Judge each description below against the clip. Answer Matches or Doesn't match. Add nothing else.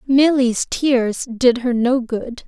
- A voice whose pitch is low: Doesn't match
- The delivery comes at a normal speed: Matches